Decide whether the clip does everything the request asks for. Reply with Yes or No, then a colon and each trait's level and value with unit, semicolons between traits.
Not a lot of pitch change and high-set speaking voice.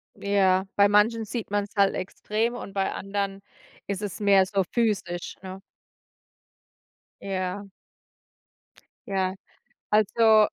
Yes: narrow, 1.6 semitones; high, 200 Hz